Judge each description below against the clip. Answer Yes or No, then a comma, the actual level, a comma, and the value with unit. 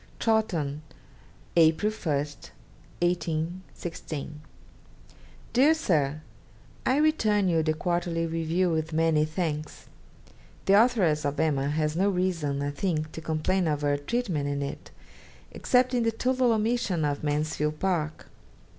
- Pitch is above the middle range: No, medium, 165 Hz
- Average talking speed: No, slow, 125 wpm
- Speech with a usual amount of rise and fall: Yes, average, 4.3 semitones